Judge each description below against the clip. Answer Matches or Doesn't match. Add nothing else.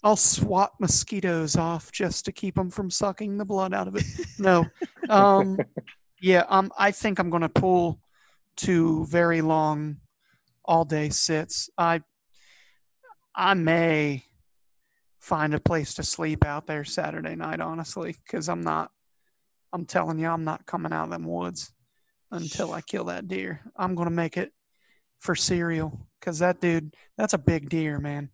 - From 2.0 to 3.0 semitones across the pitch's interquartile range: Doesn't match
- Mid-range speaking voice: Matches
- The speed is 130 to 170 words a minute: Matches